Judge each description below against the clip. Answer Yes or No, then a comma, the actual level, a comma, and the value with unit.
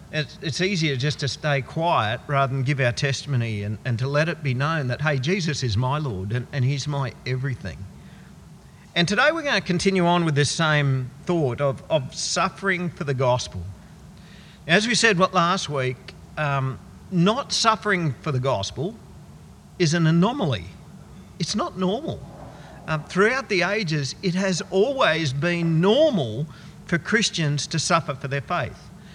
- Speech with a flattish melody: No, average, 4.8 semitones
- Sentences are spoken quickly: No, average, 165 wpm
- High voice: No, medium, 155 Hz